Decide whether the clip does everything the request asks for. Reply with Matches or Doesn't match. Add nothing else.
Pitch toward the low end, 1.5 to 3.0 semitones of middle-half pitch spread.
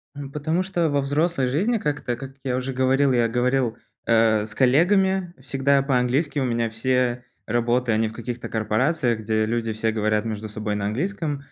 Doesn't match